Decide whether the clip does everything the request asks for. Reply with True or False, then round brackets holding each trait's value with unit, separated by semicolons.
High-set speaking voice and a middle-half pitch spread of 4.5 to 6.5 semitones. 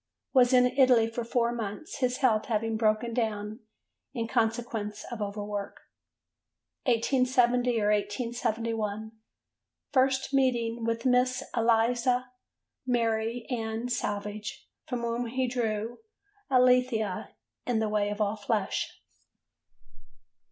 False (230 Hz; 2.5 semitones)